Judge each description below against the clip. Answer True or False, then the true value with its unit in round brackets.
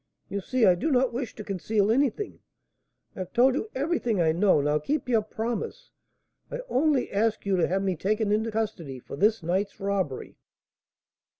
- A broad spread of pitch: False (4.6 semitones)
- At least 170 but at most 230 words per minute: True (180 wpm)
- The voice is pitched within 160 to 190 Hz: False (215 Hz)